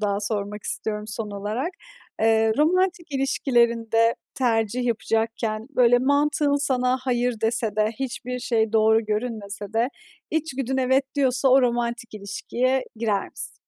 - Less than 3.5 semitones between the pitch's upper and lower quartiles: Yes, average, 3.1 semitones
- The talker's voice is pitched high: Yes, high, 235 Hz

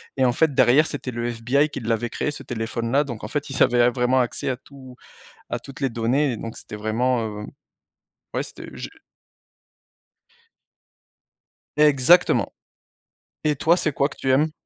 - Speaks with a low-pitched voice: Yes, low, 130 Hz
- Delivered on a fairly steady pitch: No, average, 3.2 semitones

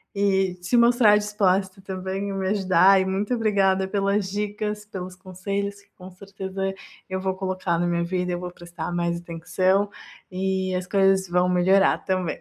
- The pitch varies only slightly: Yes, narrow, 1.6 semitones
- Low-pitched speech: No, high, 190 Hz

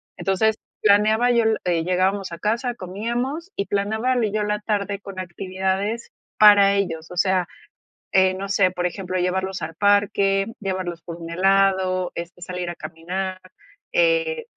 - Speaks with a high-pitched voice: Yes, high, 195 Hz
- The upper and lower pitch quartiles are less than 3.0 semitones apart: Yes, narrow, 2.4 semitones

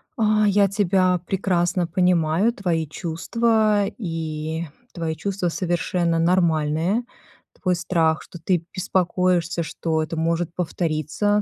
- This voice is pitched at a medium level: Yes, medium, 175 Hz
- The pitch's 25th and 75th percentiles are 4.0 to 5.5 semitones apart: No, average, 2.9 semitones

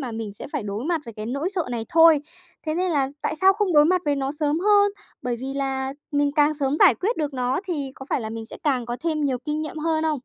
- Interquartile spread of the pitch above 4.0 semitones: No, average, 3.7 semitones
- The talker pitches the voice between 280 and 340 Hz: Yes, very high, 290 Hz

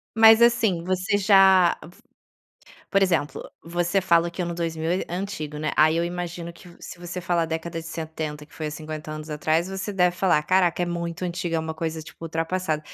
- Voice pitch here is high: No, medium, 170 Hz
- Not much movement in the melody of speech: Yes, narrow, 2.3 semitones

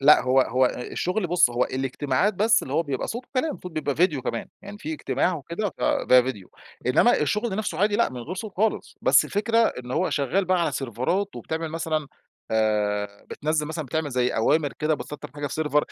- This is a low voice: No, medium, 155 Hz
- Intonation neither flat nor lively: No, wide, 6.9 semitones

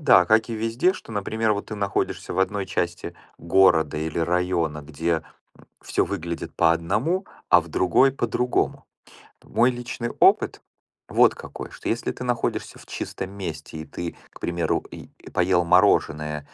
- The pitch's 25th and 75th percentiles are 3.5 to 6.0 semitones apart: Yes, average, 5.1 semitones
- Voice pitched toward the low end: Yes, very low, 90 Hz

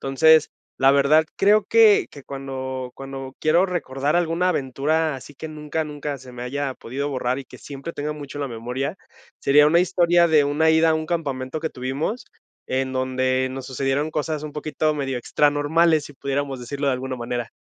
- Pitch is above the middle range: No, medium, 145 Hz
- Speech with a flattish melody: No, average, 3.1 semitones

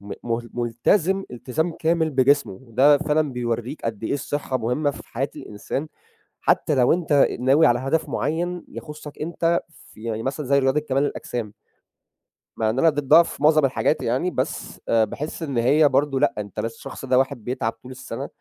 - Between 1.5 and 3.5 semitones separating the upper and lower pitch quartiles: No, average, 4.2 semitones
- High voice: No, low, 135 Hz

